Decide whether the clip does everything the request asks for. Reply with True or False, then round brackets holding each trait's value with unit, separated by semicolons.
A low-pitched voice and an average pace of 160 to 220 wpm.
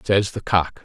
True (95 Hz; 215 wpm)